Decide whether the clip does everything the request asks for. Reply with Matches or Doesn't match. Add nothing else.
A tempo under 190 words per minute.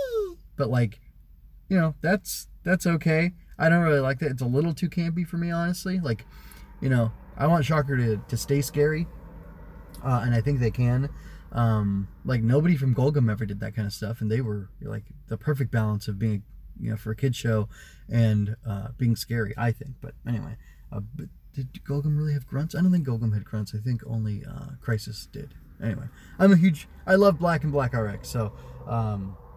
Doesn't match